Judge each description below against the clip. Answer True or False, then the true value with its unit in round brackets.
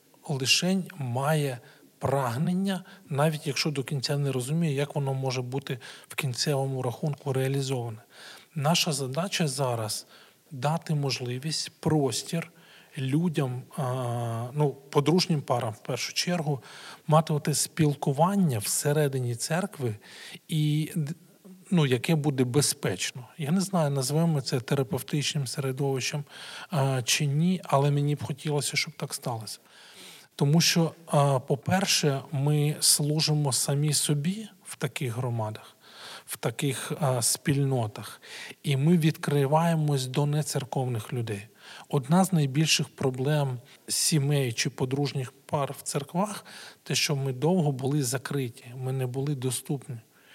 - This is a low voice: False (145 Hz)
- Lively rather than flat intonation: False (3.0 semitones)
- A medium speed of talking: True (115 wpm)